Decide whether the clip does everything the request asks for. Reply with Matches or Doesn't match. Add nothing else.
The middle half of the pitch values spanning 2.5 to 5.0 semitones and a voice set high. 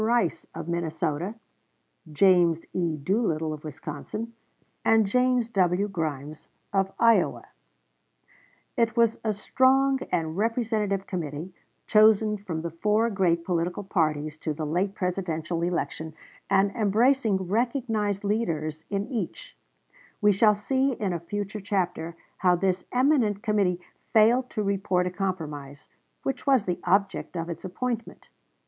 Matches